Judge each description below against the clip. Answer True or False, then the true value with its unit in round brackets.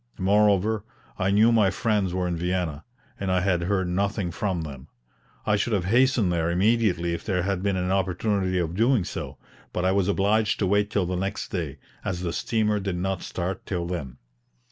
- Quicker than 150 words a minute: True (195 wpm)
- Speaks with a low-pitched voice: True (95 Hz)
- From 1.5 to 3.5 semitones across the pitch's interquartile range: True (2.7 semitones)